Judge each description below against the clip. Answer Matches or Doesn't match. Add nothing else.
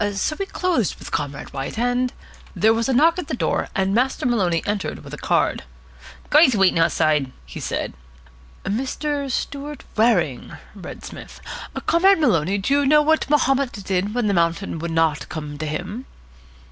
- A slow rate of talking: Doesn't match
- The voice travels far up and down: Matches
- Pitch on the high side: Matches